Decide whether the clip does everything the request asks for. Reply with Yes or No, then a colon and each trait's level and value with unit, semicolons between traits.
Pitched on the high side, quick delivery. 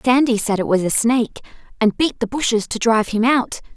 Yes: high, 230 Hz; fast, 225 wpm